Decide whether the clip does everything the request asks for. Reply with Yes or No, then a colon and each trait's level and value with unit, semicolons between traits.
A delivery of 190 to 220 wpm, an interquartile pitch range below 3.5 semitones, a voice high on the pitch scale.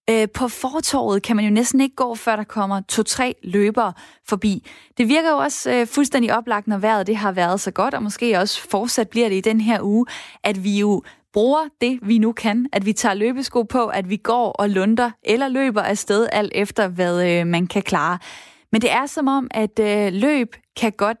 Yes: average, 205 wpm; average, 3.1 semitones; high, 220 Hz